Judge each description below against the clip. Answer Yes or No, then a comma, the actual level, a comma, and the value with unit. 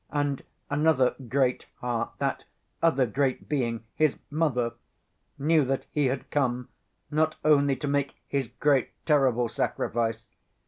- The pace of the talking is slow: Yes, slow, 130 wpm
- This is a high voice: No, low, 135 Hz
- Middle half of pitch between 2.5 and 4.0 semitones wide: Yes, average, 3.0 semitones